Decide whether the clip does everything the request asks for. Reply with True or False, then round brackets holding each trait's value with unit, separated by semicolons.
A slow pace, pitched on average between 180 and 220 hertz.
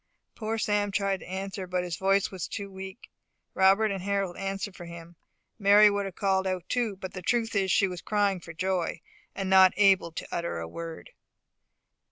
False (200 wpm; 190 Hz)